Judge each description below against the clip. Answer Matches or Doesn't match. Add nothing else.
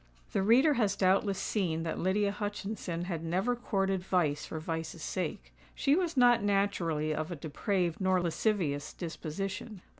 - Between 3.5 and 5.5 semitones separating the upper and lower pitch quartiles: Matches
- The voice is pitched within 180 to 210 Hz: Matches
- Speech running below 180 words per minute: Matches